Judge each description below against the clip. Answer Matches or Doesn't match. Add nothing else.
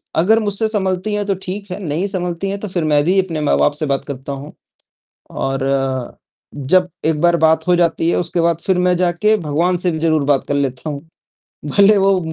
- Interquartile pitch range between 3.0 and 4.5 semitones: Matches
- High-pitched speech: Doesn't match